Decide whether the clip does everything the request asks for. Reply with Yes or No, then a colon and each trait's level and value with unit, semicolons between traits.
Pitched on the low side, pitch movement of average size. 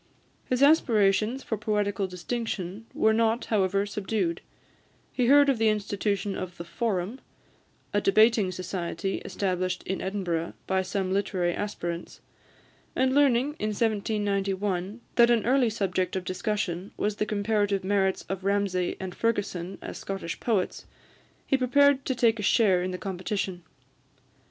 No: high, 200 Hz; average, 3.2 semitones